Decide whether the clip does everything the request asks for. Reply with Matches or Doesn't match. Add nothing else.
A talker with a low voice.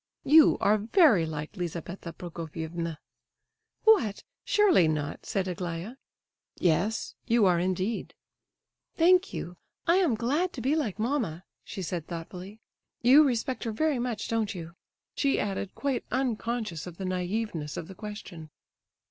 Doesn't match